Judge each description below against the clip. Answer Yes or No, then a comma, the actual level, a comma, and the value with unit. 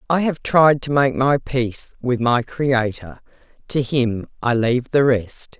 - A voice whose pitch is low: Yes, low, 125 Hz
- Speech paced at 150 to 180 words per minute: Yes, average, 170 wpm